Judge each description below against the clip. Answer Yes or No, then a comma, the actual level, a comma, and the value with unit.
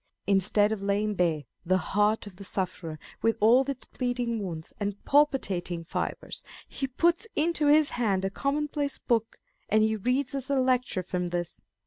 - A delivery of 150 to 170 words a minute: Yes, average, 165 wpm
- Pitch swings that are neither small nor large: No, wide, 5.9 semitones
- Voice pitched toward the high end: Yes, high, 220 Hz